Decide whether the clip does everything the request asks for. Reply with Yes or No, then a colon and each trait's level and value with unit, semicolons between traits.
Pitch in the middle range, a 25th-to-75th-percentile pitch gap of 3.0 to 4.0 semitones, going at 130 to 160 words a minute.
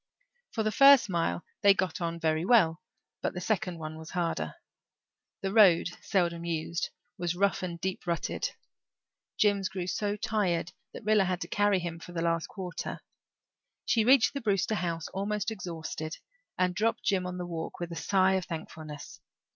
No: medium, 180 Hz; average, 3.3 semitones; average, 170 wpm